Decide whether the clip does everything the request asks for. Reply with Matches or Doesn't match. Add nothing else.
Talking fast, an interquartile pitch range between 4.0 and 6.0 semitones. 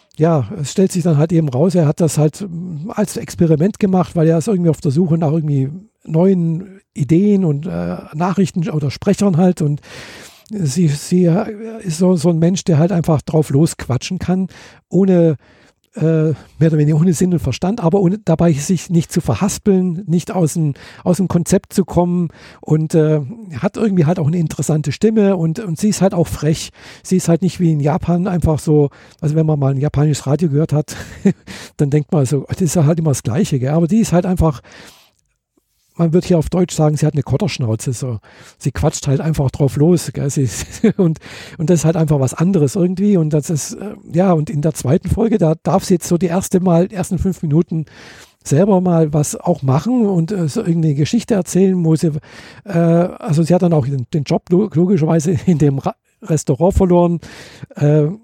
Doesn't match